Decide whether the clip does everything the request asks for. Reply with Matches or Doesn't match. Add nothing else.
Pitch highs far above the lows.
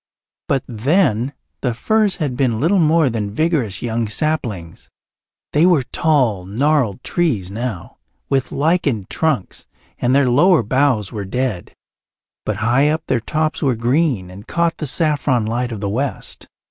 Matches